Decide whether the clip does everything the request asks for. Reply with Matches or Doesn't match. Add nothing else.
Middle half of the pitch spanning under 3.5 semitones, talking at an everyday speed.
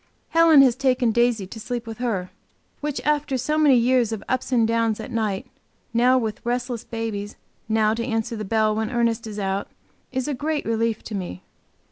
Matches